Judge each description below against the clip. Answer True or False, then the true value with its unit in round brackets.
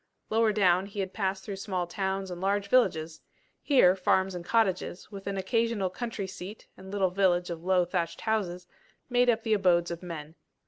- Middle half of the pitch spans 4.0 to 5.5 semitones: False (2.5 semitones)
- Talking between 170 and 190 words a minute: True (185 wpm)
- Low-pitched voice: False (190 Hz)